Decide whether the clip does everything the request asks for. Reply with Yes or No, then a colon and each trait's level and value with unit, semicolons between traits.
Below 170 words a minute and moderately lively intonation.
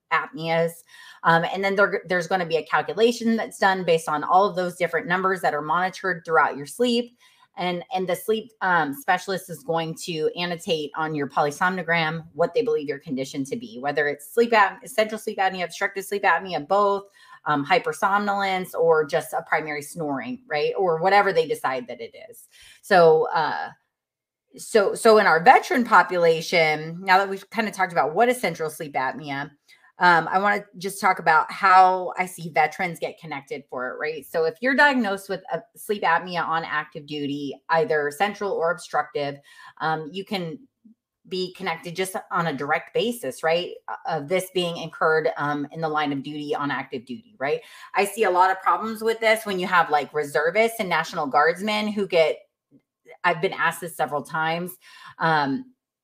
No: average, 185 wpm; average, 4.7 semitones